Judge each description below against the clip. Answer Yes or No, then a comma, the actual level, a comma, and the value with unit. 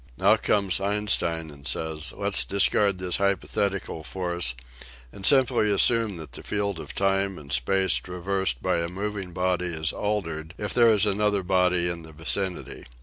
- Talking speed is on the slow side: No, average, 170 wpm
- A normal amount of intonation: Yes, average, 3.2 semitones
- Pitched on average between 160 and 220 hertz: No, very low, 95 Hz